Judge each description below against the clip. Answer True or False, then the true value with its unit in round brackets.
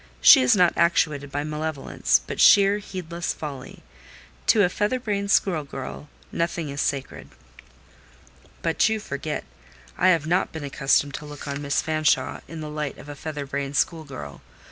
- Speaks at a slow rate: False (165 wpm)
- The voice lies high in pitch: False (155 Hz)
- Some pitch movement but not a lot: True (3.3 semitones)